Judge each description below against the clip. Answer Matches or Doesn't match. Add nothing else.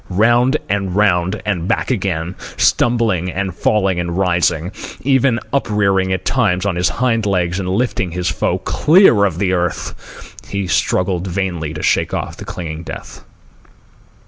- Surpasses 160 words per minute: Doesn't match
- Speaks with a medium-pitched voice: Doesn't match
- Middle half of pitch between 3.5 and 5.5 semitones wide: Doesn't match